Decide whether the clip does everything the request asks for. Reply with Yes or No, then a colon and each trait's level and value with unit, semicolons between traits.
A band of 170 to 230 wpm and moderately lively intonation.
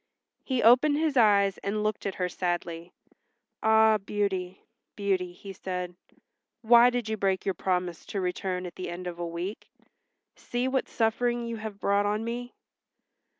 No: average, 160 wpm; average, 3.8 semitones